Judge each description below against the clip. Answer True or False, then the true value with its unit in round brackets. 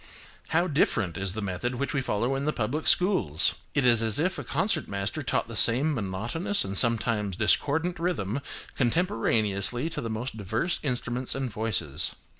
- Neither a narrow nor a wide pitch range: False (6.1 semitones)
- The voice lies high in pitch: False (120 Hz)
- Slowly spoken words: False (170 wpm)